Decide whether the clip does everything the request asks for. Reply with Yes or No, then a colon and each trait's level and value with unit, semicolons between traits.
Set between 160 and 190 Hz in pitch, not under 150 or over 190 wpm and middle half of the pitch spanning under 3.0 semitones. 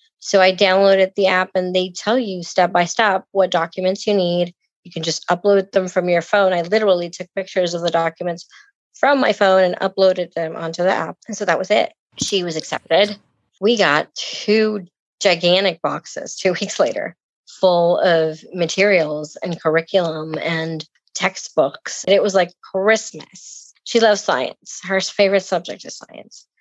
Yes: medium, 185 Hz; average, 170 wpm; narrow, 2.6 semitones